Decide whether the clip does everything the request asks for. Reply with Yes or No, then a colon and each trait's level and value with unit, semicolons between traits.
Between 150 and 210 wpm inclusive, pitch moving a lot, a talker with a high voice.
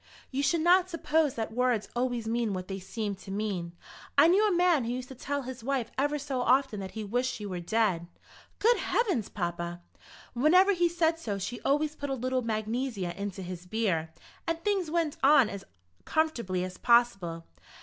Yes: average, 190 wpm; wide, 7.1 semitones; high, 240 Hz